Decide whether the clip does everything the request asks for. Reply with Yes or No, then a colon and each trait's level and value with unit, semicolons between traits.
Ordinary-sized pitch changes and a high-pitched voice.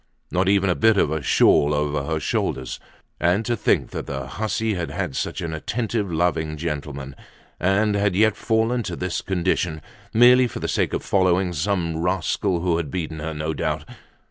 No: average, 4.5 semitones; very low, 90 Hz